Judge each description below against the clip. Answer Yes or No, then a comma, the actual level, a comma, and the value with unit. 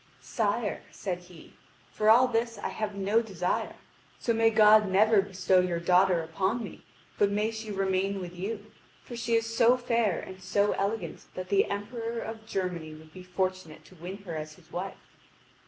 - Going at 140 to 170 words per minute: No, average, 180 wpm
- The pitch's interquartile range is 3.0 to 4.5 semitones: Yes, average, 3.3 semitones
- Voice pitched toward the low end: No, high, 200 Hz